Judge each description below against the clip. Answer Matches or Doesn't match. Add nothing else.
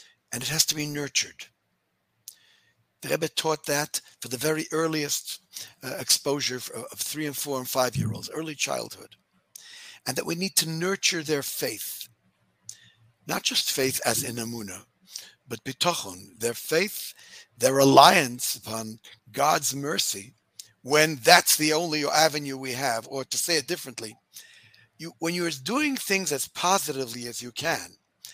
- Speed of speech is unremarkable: Matches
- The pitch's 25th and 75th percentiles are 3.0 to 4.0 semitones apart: Doesn't match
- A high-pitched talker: Doesn't match